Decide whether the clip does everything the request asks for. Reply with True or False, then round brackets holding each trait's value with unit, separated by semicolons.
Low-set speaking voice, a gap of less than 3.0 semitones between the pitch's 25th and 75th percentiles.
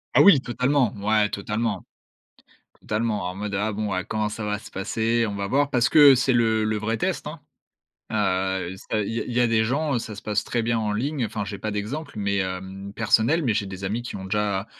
True (110 Hz; 2.6 semitones)